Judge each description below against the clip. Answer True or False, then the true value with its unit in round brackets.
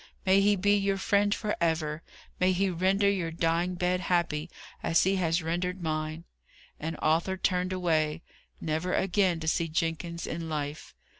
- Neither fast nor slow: True (160 wpm)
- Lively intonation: False (2.6 semitones)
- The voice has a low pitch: False (175 Hz)